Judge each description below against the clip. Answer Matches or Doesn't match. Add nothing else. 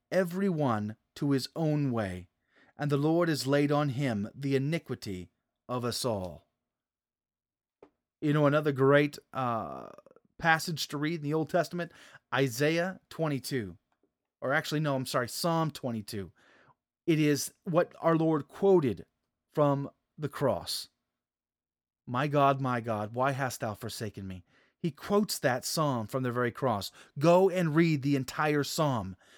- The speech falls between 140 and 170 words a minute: Matches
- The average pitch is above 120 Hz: Matches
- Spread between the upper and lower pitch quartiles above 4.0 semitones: Matches